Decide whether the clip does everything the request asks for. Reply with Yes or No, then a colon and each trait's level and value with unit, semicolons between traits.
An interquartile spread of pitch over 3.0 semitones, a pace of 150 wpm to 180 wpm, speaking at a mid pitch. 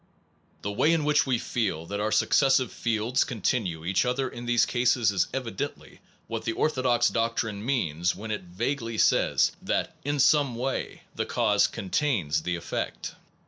No: average, 4.4 semitones; average, 165 wpm; low, 115 Hz